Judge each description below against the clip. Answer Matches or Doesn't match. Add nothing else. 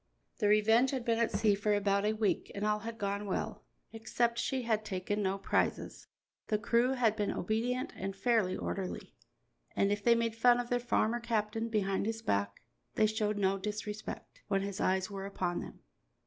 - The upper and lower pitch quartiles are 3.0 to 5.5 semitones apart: Doesn't match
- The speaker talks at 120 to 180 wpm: Doesn't match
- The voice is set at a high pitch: Matches